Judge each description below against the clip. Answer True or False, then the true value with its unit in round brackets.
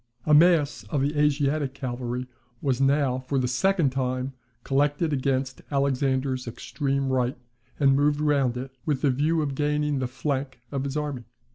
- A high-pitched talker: False (140 Hz)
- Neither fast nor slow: True (160 wpm)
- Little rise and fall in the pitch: True (2.1 semitones)